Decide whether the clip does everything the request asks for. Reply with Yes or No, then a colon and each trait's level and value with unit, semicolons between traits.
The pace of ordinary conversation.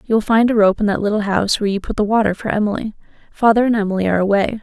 No: fast, 275 wpm